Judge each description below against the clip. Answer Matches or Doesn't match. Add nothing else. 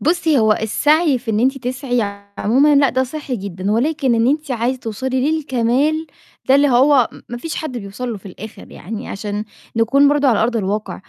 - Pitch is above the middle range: Matches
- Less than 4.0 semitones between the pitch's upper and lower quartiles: Doesn't match